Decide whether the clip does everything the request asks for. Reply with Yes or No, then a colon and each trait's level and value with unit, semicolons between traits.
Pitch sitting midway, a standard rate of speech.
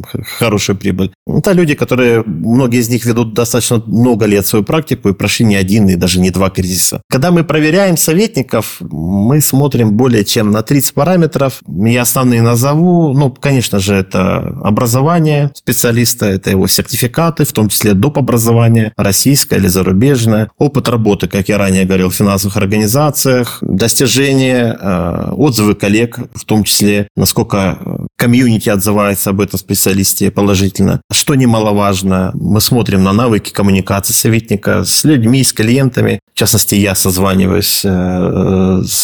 No: low, 110 Hz; average, 145 wpm